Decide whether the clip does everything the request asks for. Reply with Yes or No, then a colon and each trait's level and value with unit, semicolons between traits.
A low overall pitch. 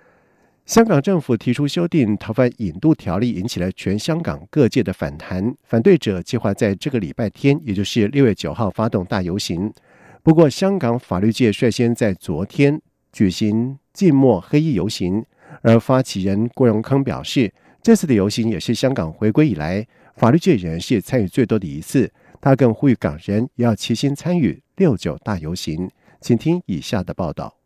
Yes: low, 120 Hz